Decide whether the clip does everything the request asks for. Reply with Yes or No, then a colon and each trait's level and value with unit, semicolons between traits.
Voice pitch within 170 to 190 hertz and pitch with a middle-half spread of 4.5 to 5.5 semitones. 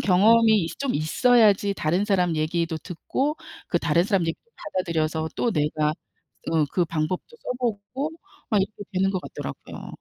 Yes: medium, 185 Hz; average, 5.1 semitones